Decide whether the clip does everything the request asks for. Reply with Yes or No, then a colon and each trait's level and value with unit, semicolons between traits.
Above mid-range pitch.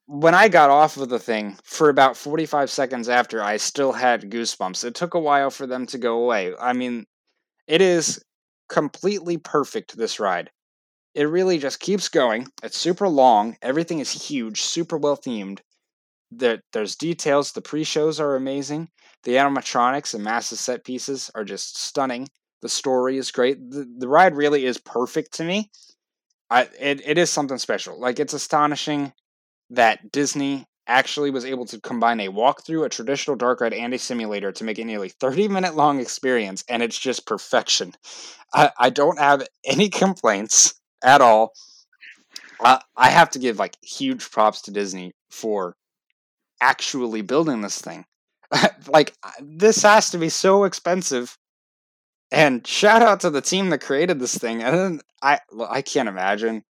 No: medium, 140 Hz